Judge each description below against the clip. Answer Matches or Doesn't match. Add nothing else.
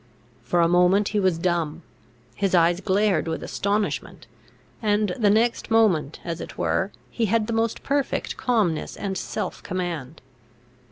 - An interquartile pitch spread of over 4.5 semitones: Doesn't match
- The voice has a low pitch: Doesn't match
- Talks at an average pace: Matches